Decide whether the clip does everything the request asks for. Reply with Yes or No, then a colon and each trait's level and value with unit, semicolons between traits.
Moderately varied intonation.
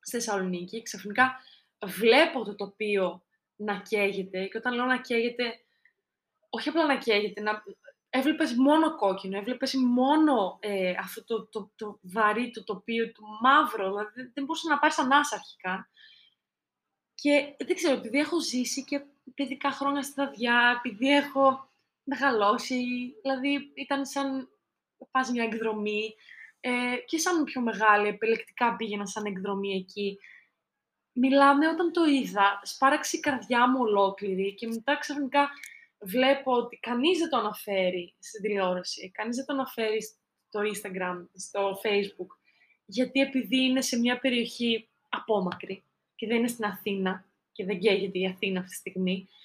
Yes: average, 5.0 semitones